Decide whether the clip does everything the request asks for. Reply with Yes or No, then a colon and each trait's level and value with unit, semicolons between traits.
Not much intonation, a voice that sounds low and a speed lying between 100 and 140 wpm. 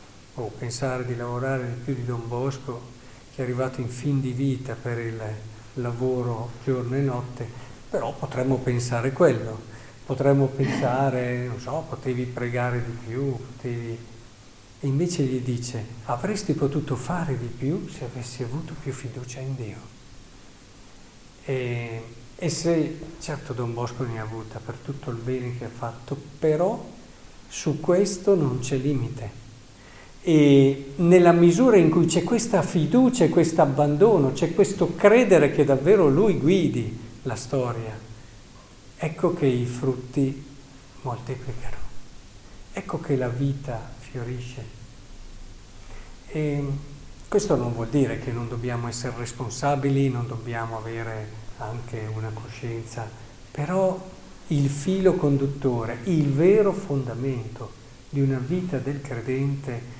No: average, 3.1 semitones; low, 125 Hz; average, 130 wpm